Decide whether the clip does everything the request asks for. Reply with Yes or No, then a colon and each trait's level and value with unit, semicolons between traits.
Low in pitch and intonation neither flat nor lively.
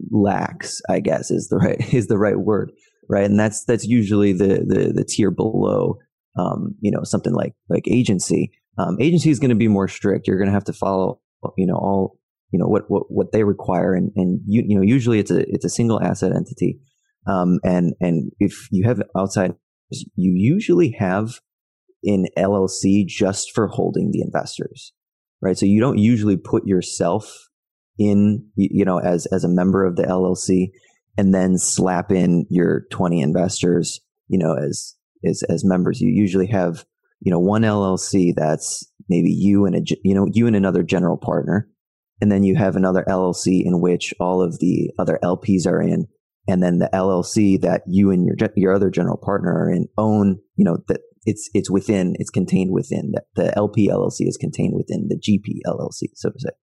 No: very low, 95 Hz; narrow, 2.3 semitones